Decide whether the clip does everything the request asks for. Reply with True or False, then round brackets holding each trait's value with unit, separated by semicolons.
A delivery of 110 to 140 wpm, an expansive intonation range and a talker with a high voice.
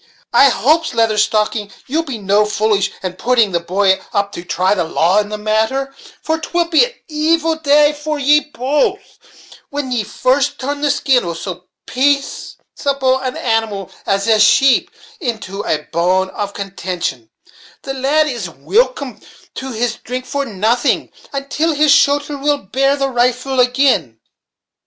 False (155 wpm; 5.8 semitones; 250 Hz)